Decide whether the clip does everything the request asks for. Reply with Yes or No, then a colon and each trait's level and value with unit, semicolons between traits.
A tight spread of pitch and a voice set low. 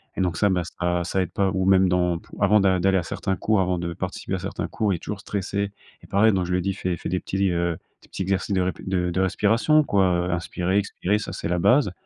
Yes: narrow, 1.9 semitones; very low, 95 Hz